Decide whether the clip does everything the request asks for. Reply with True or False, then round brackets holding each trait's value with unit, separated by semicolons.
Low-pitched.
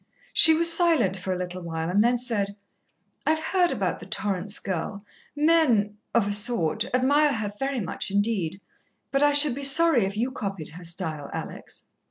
False (215 Hz)